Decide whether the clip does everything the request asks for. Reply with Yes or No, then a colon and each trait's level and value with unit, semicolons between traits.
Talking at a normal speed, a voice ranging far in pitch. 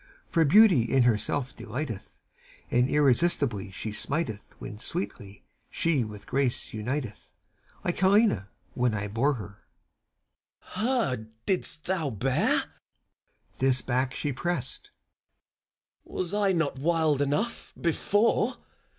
No: slow, 120 wpm; wide, 7.1 semitones